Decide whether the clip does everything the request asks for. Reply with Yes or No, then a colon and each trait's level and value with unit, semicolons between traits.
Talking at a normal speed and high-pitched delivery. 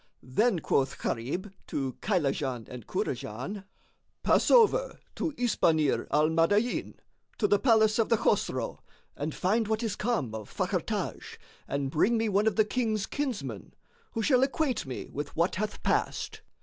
Yes: average, 155 wpm; high, 205 Hz